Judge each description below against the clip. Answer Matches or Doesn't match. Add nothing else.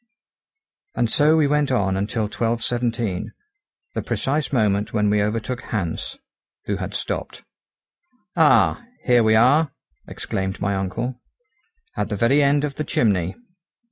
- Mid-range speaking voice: Doesn't match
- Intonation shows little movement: Doesn't match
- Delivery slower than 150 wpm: Matches